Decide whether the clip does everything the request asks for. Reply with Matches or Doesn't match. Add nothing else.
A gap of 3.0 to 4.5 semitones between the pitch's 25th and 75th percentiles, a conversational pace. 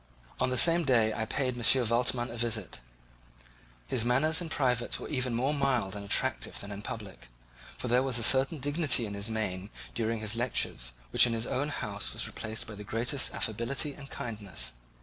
Matches